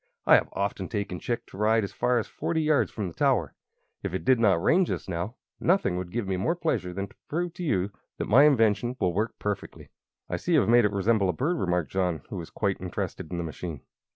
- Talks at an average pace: No, fast, 240 wpm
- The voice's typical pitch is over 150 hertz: No, low, 105 Hz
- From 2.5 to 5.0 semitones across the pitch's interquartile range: No, wide, 5.5 semitones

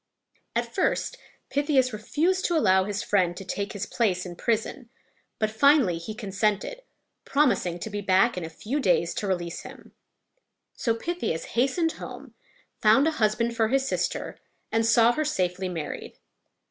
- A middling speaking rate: Yes, average, 160 wpm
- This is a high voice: Yes, high, 215 Hz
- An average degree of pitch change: No, wide, 6.2 semitones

